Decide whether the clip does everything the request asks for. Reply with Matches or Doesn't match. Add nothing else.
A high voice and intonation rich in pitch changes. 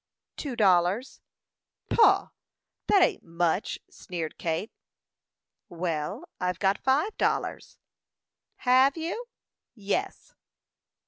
Matches